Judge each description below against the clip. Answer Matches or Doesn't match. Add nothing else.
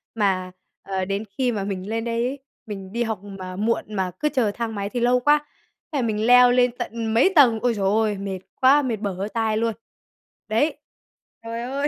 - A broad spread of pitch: Doesn't match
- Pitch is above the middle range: Matches